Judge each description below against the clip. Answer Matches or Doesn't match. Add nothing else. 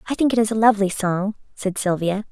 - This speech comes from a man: Doesn't match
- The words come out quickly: Matches